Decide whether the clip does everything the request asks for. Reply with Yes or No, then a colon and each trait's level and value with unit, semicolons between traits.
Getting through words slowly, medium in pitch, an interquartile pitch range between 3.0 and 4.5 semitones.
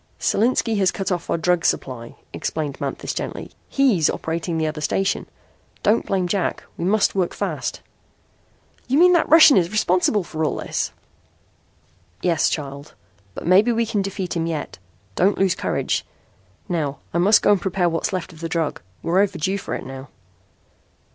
No: average, 165 wpm; medium, 180 Hz; average, 3.7 semitones